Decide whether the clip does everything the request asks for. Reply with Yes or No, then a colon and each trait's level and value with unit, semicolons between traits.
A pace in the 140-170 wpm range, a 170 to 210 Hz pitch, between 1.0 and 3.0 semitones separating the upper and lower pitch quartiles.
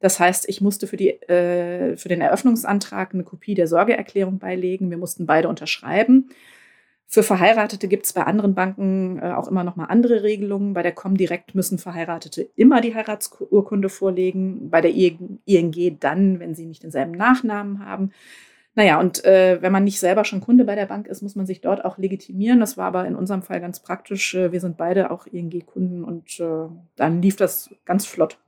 No: fast, 190 wpm; high, 190 Hz; narrow, 2.5 semitones